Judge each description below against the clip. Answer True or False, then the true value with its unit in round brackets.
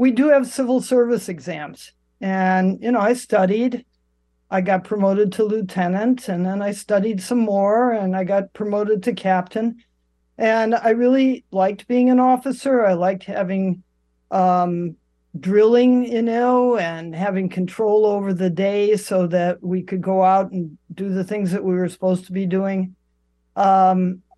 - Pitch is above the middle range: True (195 Hz)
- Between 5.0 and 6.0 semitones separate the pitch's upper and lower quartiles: False (3.5 semitones)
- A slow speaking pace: False (160 wpm)